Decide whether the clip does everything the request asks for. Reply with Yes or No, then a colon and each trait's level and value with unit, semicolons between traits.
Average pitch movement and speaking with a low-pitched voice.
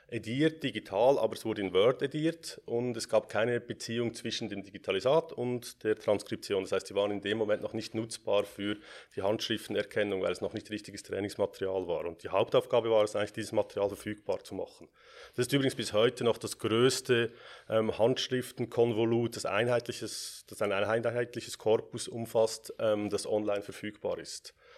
No: narrow, 2.3 semitones; low, 110 Hz